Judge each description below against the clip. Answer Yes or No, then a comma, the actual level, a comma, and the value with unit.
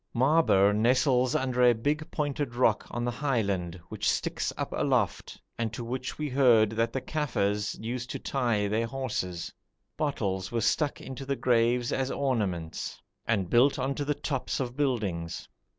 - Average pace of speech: Yes, average, 165 wpm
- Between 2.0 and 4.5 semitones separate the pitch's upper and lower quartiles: Yes, average, 4.0 semitones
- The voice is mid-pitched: No, low, 120 Hz